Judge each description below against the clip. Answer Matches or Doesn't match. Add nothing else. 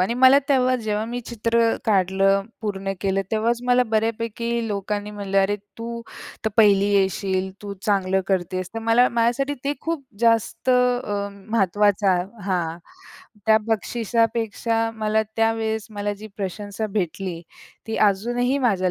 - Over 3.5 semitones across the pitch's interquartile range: Doesn't match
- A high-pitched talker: Matches